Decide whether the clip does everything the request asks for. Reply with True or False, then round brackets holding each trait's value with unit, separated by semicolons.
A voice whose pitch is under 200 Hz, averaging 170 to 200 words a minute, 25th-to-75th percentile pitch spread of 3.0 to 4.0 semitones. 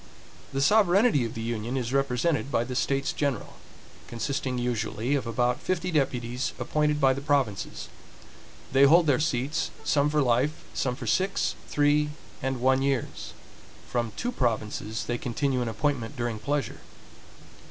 False (135 Hz; 150 wpm; 3.3 semitones)